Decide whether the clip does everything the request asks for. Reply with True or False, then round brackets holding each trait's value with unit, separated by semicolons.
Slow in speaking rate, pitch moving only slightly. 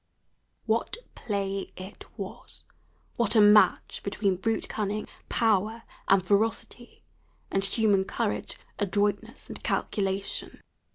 True (105 wpm; 2.2 semitones)